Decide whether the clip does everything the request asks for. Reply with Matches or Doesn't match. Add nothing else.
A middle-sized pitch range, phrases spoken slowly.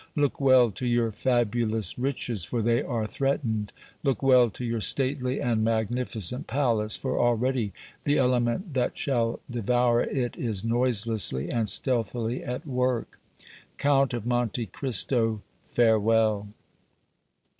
Doesn't match